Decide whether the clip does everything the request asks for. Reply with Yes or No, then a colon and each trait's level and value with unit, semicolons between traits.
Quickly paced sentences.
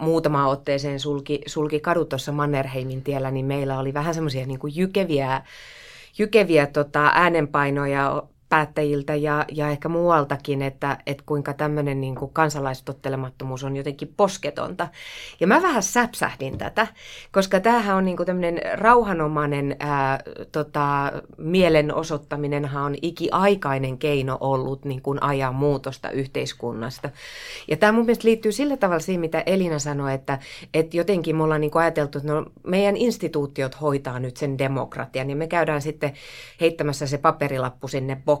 No: average, 140 wpm